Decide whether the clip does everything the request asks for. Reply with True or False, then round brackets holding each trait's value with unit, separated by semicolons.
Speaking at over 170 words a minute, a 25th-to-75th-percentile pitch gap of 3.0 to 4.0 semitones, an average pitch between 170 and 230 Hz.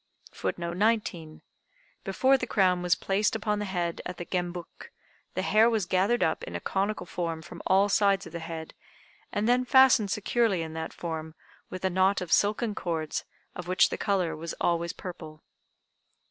True (180 wpm; 3.6 semitones; 185 Hz)